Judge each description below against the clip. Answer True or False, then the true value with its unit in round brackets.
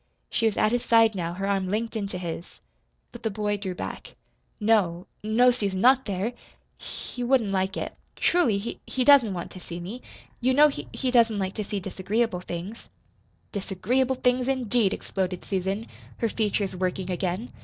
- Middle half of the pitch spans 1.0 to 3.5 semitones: False (4.1 semitones)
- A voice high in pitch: True (210 Hz)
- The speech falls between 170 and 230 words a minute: True (180 wpm)